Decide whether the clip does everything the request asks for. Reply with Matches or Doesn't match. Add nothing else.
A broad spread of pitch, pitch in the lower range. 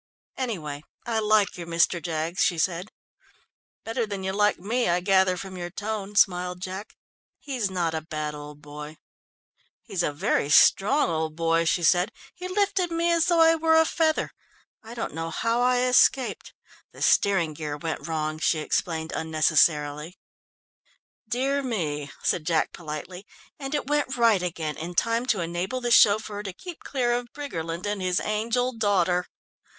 Doesn't match